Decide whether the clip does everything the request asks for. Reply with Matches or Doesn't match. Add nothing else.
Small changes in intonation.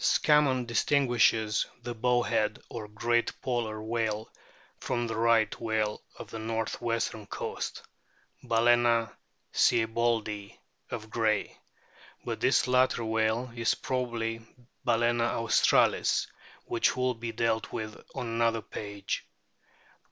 Matches